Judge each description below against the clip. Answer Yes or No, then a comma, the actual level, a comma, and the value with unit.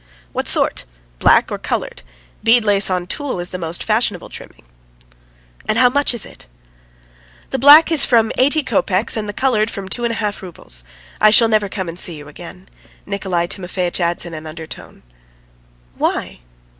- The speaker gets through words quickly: No, average, 170 wpm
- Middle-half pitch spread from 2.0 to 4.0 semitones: No, average, 4.8 semitones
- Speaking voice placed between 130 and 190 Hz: No, high, 200 Hz